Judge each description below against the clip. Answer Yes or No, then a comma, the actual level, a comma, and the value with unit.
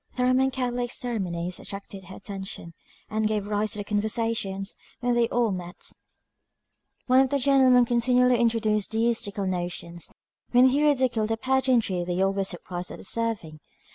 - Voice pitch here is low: No, high, 220 Hz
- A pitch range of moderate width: Yes, average, 4.2 semitones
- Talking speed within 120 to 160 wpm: Yes, average, 155 wpm